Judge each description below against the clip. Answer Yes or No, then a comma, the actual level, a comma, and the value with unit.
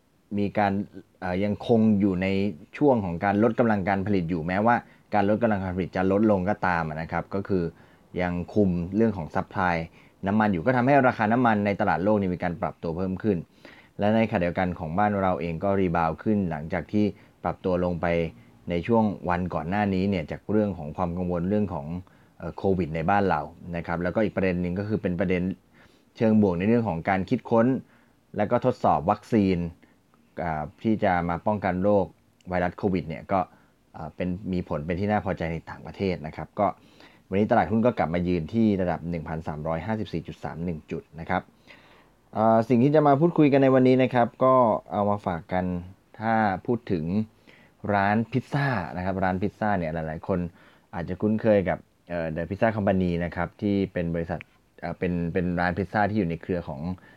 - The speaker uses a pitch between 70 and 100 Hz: Yes, very low, 95 Hz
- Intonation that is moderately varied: Yes, average, 3.4 semitones